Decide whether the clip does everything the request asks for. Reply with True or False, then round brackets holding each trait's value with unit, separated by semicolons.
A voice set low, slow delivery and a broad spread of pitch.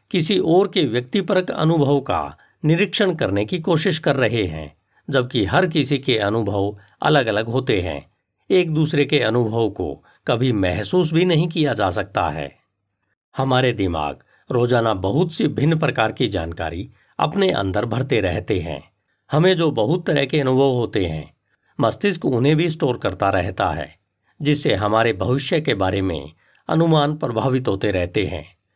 False (130 Hz; 155 wpm; 7.8 semitones)